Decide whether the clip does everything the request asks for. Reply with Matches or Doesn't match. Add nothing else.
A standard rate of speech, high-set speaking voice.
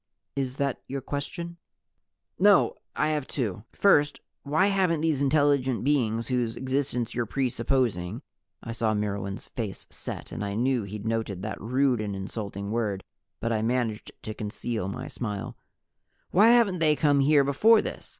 Doesn't match